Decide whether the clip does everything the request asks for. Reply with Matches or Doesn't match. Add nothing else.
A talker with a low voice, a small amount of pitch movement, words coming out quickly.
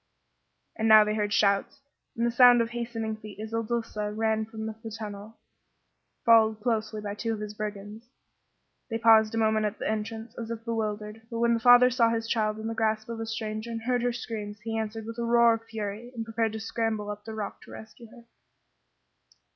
Doesn't match